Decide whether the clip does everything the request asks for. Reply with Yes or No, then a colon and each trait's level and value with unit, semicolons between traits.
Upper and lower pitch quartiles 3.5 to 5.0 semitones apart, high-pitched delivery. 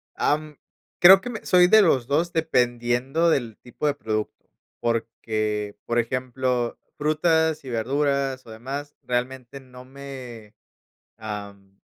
No: average, 4.1 semitones; low, 130 Hz